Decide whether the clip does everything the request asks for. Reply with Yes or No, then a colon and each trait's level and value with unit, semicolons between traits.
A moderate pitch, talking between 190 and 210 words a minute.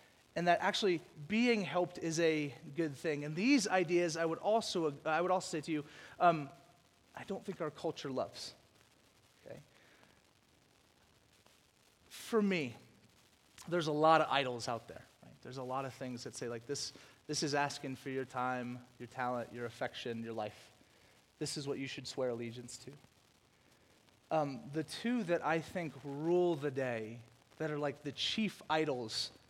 No: medium, 150 Hz; average, 170 wpm